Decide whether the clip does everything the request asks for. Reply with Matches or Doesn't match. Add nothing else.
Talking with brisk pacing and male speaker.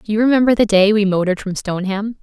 Doesn't match